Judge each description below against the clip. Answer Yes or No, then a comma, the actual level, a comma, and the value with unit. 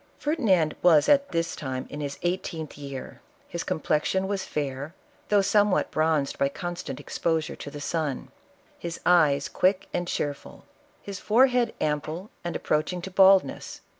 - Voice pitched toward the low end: No, medium, 170 Hz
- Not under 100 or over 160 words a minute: Yes, average, 155 wpm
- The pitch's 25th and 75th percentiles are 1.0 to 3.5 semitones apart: No, average, 4.3 semitones